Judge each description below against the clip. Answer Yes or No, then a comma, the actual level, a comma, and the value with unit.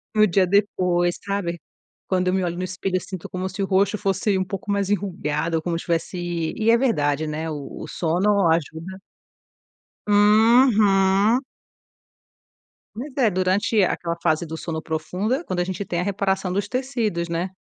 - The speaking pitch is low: No, medium, 185 Hz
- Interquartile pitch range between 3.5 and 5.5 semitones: No, average, 3.1 semitones